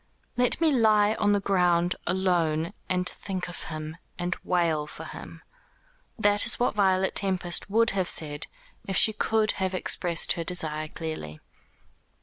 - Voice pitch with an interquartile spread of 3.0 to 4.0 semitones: Yes, average, 3.6 semitones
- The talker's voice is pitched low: No, medium, 185 Hz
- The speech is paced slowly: No, average, 150 wpm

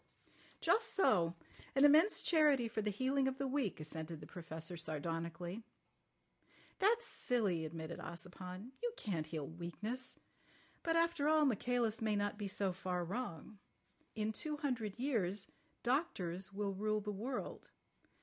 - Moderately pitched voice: No, high, 210 Hz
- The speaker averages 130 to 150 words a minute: Yes, average, 140 wpm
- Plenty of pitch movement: Yes, wide, 7.2 semitones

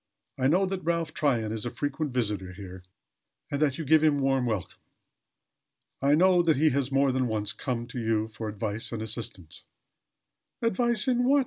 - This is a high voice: No, low, 130 Hz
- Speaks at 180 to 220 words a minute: Yes, average, 190 wpm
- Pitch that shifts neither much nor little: No, wide, 6.2 semitones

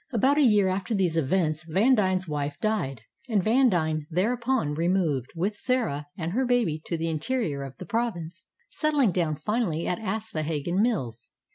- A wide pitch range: Yes, wide, 6.4 semitones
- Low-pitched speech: No, medium, 185 Hz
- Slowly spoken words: No, average, 155 wpm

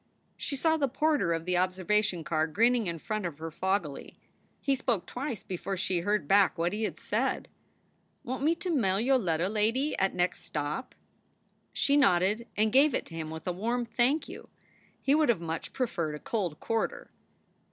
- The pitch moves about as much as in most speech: No, wide, 6.3 semitones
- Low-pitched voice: No, high, 205 Hz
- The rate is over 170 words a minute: Yes, average, 190 wpm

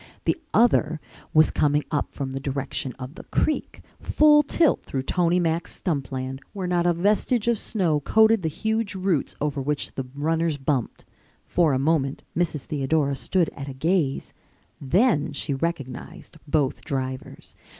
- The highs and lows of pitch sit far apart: No, average, 4.7 semitones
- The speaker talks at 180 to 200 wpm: No, average, 160 wpm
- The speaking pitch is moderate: Yes, medium, 155 Hz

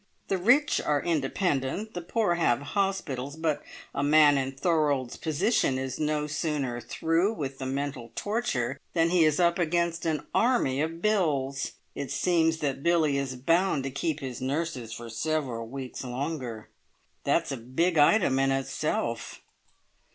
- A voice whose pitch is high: No, medium, 150 Hz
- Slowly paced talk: No, average, 150 wpm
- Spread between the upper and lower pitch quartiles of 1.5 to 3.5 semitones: No, average, 4.2 semitones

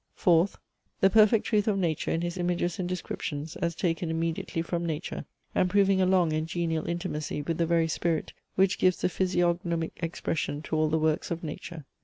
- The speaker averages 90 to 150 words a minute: No, average, 190 wpm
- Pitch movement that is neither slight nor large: No, narrow, 2.1 semitones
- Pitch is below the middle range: No, medium, 170 Hz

